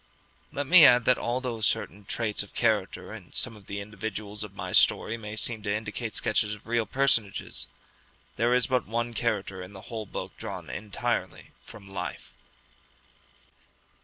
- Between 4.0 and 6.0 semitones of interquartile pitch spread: No, average, 2.7 semitones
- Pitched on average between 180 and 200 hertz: No, low, 110 Hz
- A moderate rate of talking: Yes, average, 160 wpm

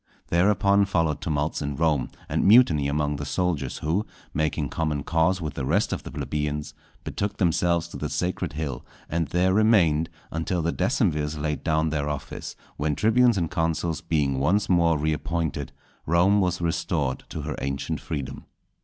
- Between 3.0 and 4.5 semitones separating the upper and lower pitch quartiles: Yes, average, 3.3 semitones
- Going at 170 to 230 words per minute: No, average, 160 wpm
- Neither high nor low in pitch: No, very low, 80 Hz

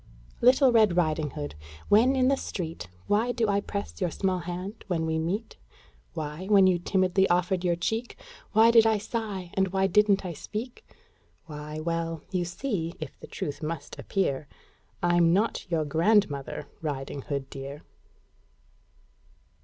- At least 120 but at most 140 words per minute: No, average, 155 wpm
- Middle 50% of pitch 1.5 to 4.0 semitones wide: No, average, 4.5 semitones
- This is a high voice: No, medium, 180 Hz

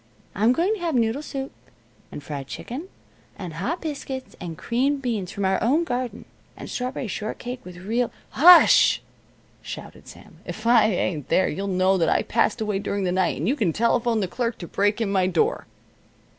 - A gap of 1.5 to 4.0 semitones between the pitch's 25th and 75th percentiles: No, average, 5.3 semitones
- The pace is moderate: Yes, average, 190 wpm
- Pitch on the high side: Yes, high, 220 Hz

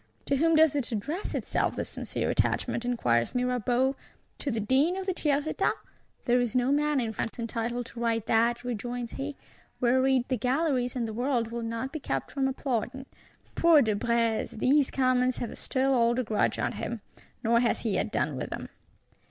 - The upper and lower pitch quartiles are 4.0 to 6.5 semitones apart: No, average, 2.7 semitones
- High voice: Yes, high, 245 Hz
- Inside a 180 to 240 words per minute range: Yes, average, 185 wpm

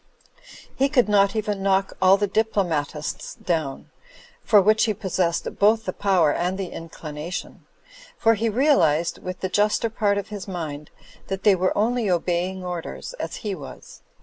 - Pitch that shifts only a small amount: No, average, 3.4 semitones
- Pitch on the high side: Yes, high, 195 Hz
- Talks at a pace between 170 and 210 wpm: No, average, 160 wpm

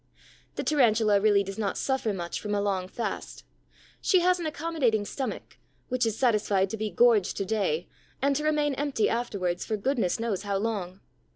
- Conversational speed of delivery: Yes, average, 180 wpm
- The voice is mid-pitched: No, high, 220 Hz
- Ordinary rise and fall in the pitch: Yes, average, 4.9 semitones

